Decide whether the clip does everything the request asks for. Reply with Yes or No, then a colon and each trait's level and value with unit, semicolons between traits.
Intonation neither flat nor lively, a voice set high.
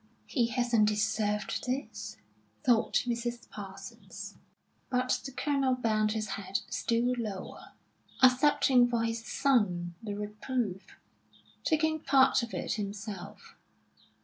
Yes: average, 3.4 semitones; high, 230 Hz